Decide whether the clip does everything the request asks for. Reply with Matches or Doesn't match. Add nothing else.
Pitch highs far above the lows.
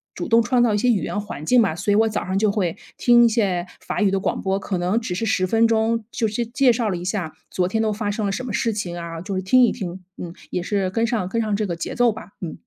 Doesn't match